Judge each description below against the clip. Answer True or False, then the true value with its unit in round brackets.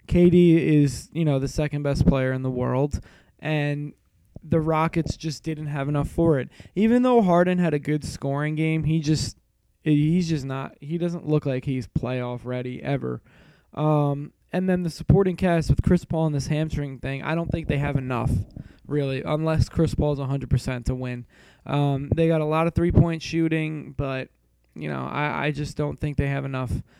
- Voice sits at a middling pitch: True (145 Hz)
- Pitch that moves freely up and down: False (3.5 semitones)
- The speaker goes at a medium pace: True (190 wpm)